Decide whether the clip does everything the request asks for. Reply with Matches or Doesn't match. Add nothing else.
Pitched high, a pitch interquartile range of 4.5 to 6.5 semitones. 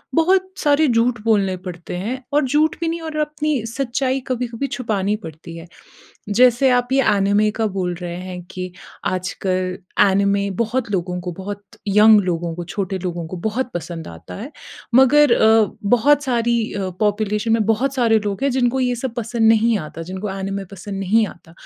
Matches